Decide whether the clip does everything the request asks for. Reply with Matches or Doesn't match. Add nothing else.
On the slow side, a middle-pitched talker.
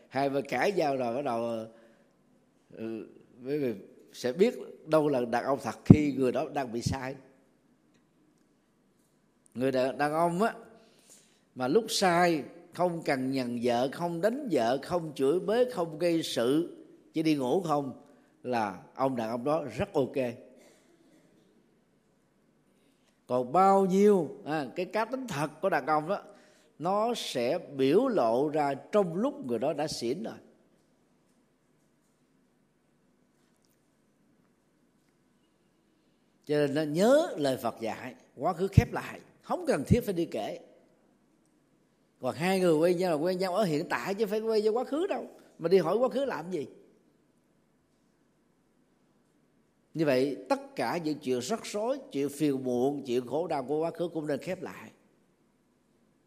Matches